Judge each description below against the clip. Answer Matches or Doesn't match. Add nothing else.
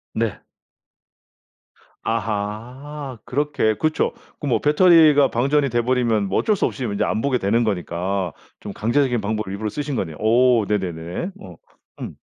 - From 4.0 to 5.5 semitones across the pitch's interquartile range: Matches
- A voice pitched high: Doesn't match